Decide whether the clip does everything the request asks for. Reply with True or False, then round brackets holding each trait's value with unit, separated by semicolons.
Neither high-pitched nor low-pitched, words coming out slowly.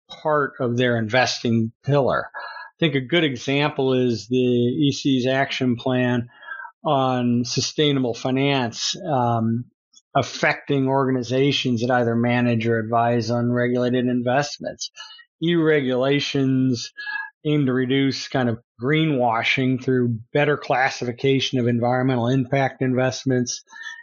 False (130 Hz; 110 wpm)